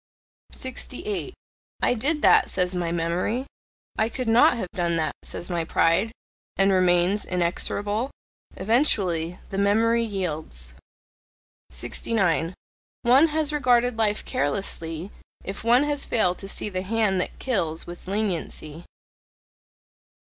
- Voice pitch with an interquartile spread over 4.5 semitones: Yes, average, 5.0 semitones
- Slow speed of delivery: Yes, slow, 120 wpm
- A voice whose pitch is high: Yes, high, 195 Hz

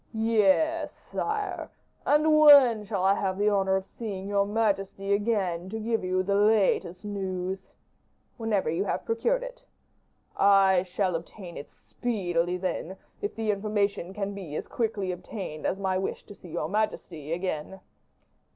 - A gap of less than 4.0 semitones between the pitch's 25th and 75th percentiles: Yes, average, 2.9 semitones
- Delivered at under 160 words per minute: Yes, average, 150 wpm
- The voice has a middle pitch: No, high, 200 Hz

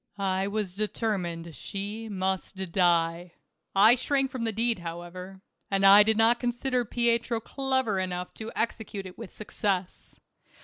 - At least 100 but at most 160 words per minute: Yes, average, 140 wpm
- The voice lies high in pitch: Yes, high, 200 Hz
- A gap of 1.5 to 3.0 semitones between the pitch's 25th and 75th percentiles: No, average, 3.8 semitones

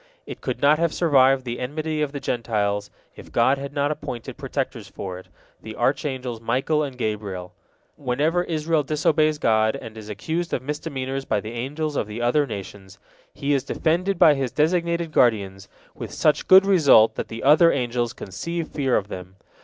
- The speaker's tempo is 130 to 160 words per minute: No, average, 175 wpm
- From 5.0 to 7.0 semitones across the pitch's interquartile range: Yes, wide, 5.5 semitones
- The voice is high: No, low, 135 Hz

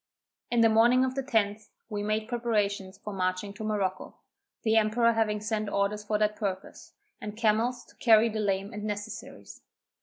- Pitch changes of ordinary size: No, narrow, 1.7 semitones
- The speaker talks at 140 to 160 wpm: No, average, 175 wpm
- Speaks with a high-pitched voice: Yes, high, 215 Hz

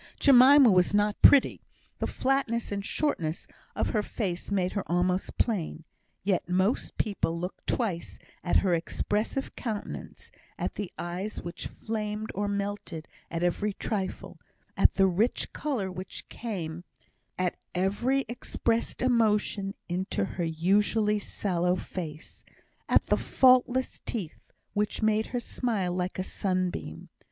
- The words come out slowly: Yes, slow, 130 wpm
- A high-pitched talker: Yes, high, 200 Hz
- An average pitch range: Yes, average, 3.8 semitones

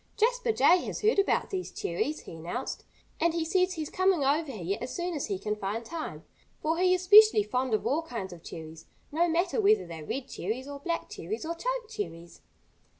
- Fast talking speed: Yes, fast, 210 wpm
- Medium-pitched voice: No, very high, 320 Hz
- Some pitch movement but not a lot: No, wide, 8.8 semitones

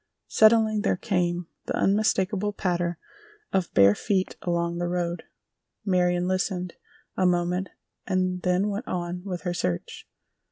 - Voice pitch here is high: No, medium, 180 Hz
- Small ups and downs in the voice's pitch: Yes, narrow, 1.8 semitones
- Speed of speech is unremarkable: No, slow, 130 wpm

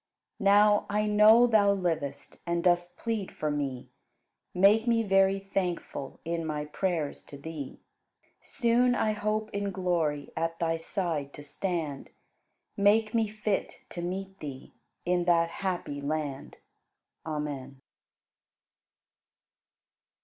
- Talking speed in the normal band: No, slow, 120 wpm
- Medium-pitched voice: Yes, medium, 180 Hz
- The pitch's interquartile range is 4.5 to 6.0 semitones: Yes, average, 5.1 semitones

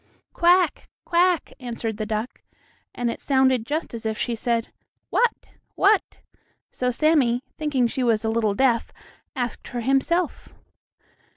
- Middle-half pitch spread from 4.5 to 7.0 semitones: Yes, average, 4.9 semitones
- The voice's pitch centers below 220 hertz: No, very high, 250 Hz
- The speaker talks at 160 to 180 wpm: No, slow, 135 wpm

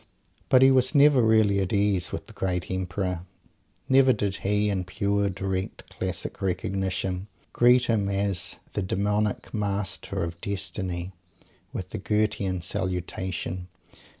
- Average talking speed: No, slow, 130 wpm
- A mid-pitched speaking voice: No, low, 100 Hz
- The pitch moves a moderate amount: No, narrow, 2.3 semitones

